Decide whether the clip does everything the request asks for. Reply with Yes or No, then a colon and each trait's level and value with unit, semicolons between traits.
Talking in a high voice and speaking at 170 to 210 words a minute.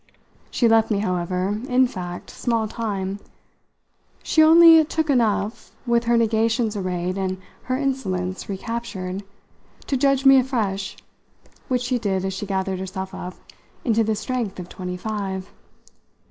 No: high, 215 Hz; average, 140 wpm